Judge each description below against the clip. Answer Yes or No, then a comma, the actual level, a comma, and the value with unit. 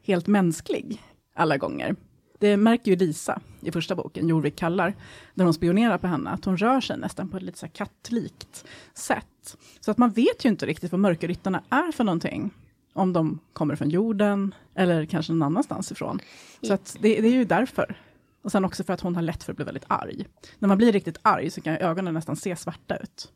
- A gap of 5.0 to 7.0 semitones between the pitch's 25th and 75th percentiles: No, average, 3.8 semitones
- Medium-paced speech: No, fast, 215 wpm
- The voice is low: No, high, 190 Hz